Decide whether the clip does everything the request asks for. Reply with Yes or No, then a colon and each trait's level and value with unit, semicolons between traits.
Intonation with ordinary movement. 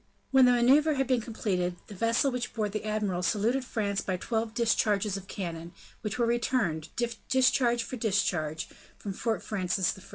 Yes: average, 3.9 semitones